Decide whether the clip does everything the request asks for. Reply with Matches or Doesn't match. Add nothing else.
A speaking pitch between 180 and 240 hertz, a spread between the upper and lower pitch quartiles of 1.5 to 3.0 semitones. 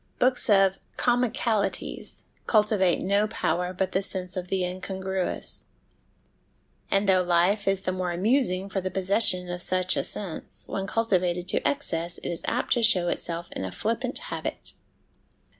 Matches